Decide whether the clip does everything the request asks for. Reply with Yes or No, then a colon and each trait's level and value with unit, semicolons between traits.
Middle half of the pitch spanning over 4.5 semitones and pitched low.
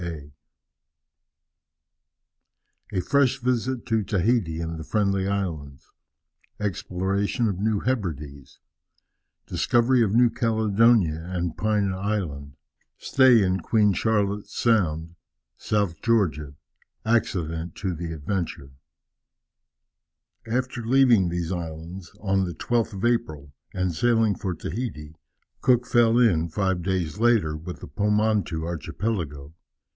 Yes: average, 5.3 semitones; low, 100 Hz